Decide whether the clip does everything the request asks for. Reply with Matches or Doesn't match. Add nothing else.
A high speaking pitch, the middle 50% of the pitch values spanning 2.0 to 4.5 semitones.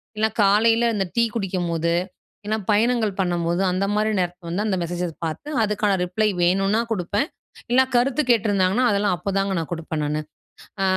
Matches